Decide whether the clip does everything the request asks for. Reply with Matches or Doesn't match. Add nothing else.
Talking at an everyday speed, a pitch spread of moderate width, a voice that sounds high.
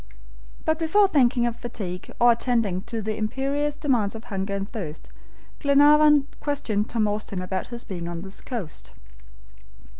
Doesn't match